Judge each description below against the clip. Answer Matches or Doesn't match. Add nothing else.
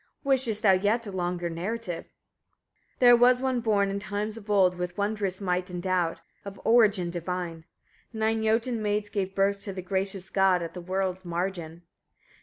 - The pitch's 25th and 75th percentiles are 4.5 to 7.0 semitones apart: Doesn't match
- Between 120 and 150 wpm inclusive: Doesn't match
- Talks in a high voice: Matches